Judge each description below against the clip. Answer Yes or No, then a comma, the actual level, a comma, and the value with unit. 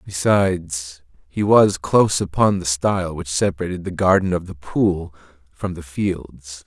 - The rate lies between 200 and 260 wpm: No, average, 155 wpm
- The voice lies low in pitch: Yes, very low, 85 Hz